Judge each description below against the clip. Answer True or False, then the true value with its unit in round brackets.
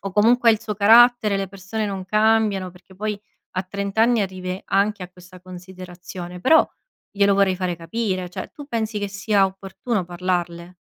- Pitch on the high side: True (195 Hz)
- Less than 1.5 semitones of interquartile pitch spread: False (2.7 semitones)